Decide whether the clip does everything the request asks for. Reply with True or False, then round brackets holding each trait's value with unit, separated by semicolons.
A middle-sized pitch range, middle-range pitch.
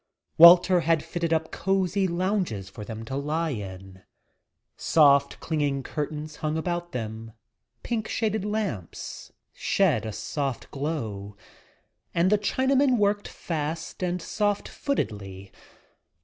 False (8.2 semitones; 160 Hz)